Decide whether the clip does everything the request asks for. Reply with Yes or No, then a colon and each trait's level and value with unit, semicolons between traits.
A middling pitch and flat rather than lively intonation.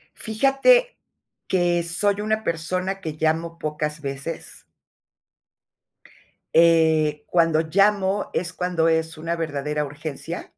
No: medium, 165 Hz; average, 3.3 semitones